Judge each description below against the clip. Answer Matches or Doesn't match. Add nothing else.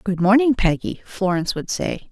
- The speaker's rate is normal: Matches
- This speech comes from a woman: Matches